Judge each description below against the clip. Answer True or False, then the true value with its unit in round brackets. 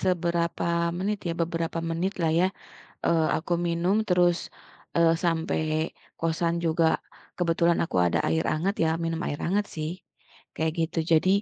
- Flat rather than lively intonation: True (1.4 semitones)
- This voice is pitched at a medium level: True (170 Hz)